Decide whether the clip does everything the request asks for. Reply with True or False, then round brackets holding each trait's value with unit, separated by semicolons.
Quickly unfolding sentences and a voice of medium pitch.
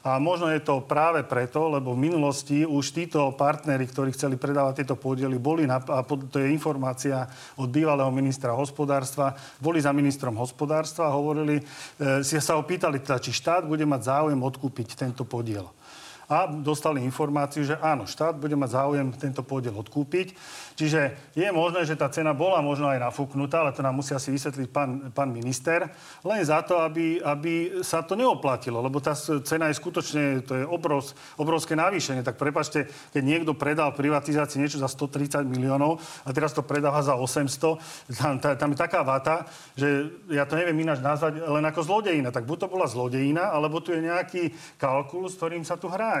True (180 wpm; 145 Hz)